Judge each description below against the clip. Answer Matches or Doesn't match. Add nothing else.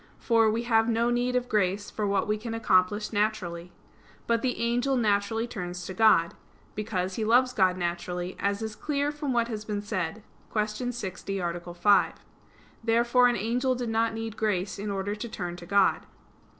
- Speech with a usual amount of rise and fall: Matches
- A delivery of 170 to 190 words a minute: Matches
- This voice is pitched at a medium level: Doesn't match